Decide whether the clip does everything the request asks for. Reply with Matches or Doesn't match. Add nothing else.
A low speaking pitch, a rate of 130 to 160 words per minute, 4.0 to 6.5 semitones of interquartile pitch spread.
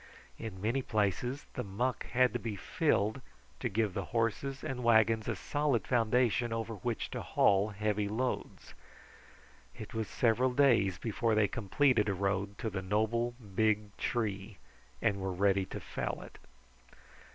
Doesn't match